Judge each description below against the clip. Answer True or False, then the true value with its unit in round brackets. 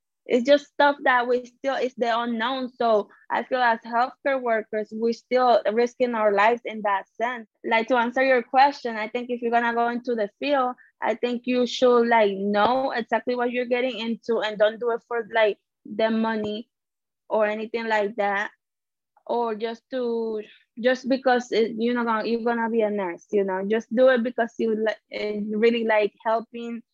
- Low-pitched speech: False (235 Hz)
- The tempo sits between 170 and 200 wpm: True (190 wpm)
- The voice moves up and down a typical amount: False (2.2 semitones)